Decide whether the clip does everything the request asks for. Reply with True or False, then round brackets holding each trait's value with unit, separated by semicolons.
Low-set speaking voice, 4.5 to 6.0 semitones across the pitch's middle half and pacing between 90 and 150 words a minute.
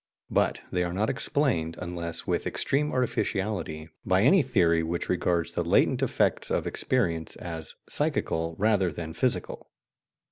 True (90 Hz; 5.0 semitones; 140 wpm)